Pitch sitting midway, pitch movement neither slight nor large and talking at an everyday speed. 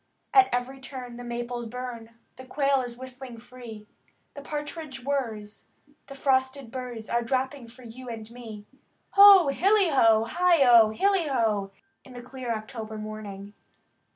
No: very high, 250 Hz; average, 3.3 semitones; average, 155 wpm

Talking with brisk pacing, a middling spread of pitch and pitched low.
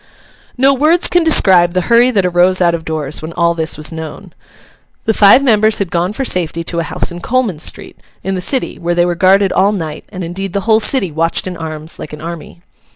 No: fast, 225 wpm; average, 3.8 semitones; medium, 180 Hz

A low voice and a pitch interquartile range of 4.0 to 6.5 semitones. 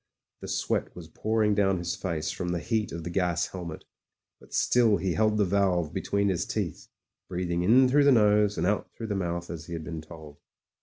No: very low, 90 Hz; average, 3.5 semitones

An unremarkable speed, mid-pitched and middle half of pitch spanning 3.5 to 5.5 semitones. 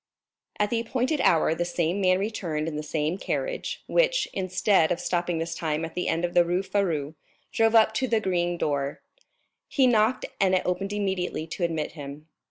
Yes: average, 190 wpm; medium, 180 Hz; average, 4.2 semitones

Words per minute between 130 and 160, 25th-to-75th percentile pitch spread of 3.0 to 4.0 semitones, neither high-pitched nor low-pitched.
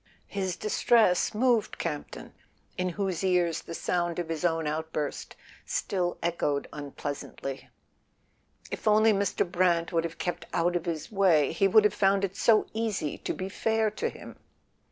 Yes: average, 155 wpm; average, 3.5 semitones; medium, 180 Hz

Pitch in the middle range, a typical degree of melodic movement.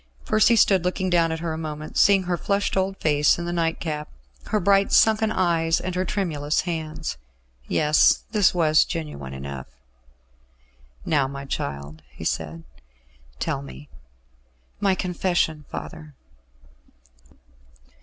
Yes: medium, 165 Hz; average, 4.0 semitones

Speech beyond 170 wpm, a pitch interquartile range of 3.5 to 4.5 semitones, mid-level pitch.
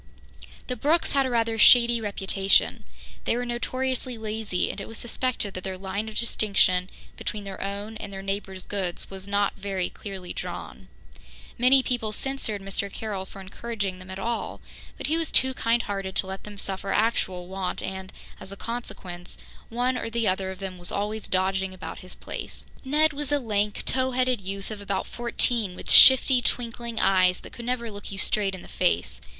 No: average, 190 wpm; average, 3.8 semitones; high, 205 Hz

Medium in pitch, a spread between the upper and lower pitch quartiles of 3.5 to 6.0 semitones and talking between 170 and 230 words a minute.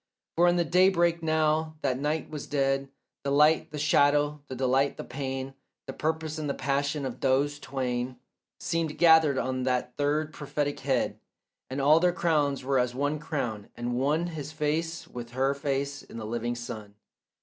No: medium, 145 Hz; average, 3.0 semitones; average, 175 wpm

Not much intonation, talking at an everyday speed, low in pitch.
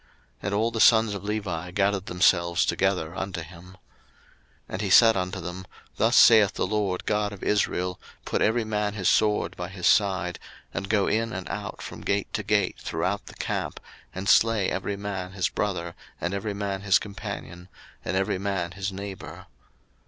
Yes: narrow, 2.2 semitones; average, 180 wpm; very low, 95 Hz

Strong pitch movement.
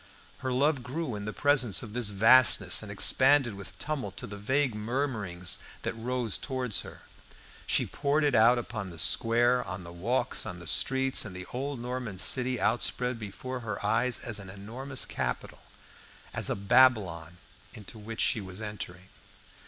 No: average, 4.3 semitones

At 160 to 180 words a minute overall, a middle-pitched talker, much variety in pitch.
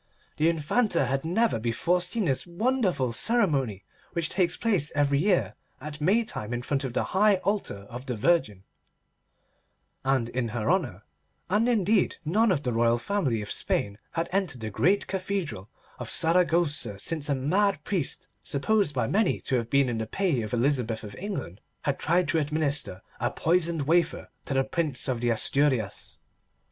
Yes: average, 170 wpm; medium, 150 Hz; wide, 6.9 semitones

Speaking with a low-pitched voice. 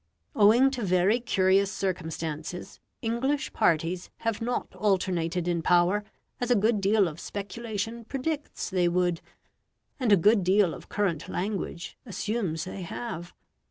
No: high, 195 Hz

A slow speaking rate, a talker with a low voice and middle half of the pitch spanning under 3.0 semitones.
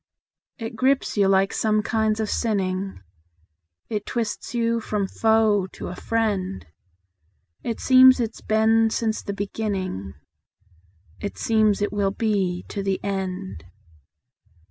No: slow, 125 wpm; high, 210 Hz; narrow, 2.5 semitones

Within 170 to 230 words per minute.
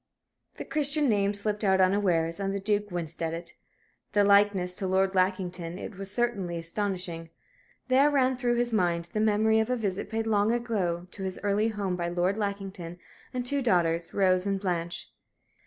Yes: average, 180 wpm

